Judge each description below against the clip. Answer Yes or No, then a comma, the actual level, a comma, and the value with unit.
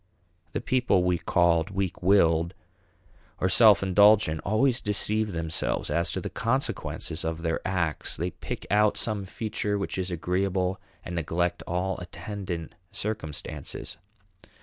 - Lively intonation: No, average, 3.3 semitones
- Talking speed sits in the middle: No, slow, 130 wpm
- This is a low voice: Yes, very low, 95 Hz